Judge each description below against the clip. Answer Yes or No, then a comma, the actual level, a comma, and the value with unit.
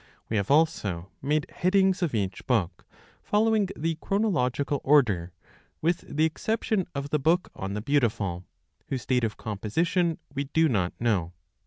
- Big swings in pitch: Yes, wide, 8.0 semitones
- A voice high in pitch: No, medium, 140 Hz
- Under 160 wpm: Yes, average, 150 wpm